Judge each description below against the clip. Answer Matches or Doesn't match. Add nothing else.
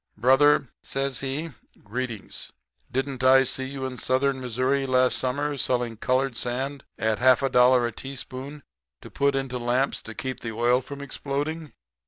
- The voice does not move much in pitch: Matches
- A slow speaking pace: Doesn't match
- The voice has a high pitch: Doesn't match